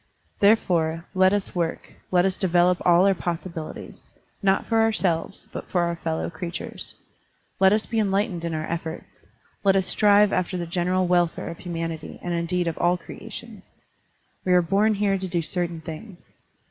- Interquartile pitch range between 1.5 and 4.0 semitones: Yes, narrow, 2.4 semitones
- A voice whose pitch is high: No, medium, 180 Hz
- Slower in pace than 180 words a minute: Yes, average, 170 wpm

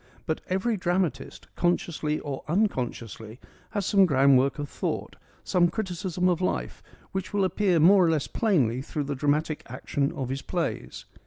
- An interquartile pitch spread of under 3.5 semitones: No, average, 5.1 semitones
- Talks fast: No, average, 155 wpm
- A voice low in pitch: No, medium, 160 Hz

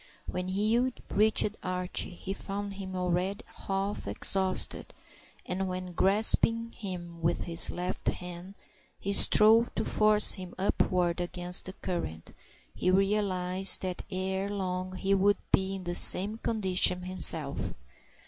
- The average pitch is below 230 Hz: Yes, high, 190 Hz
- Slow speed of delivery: Yes, slow, 130 wpm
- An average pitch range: No, narrow, 1.8 semitones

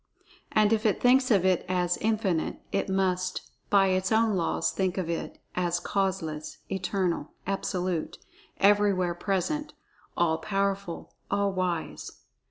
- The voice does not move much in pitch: Yes, narrow, 2.2 semitones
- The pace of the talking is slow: Yes, slow, 130 wpm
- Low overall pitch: No, high, 190 Hz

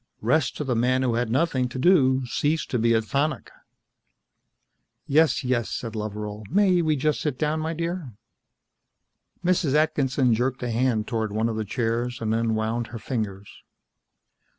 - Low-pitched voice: Yes, low, 125 Hz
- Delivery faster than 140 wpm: Yes, average, 165 wpm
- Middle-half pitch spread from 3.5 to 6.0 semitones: Yes, average, 4.8 semitones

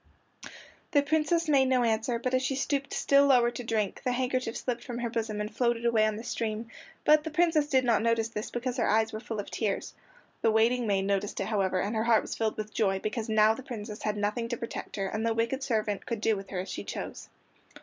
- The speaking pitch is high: Yes, high, 230 Hz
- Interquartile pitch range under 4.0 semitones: Yes, average, 2.9 semitones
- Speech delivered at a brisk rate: Yes, fast, 240 wpm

